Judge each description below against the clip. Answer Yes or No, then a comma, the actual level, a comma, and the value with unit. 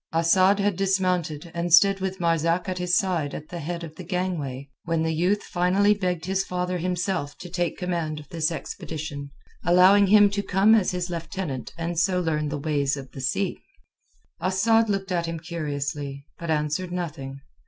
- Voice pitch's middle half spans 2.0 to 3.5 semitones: Yes, average, 3.2 semitones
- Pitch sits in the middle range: Yes, medium, 175 Hz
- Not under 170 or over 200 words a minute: Yes, average, 180 wpm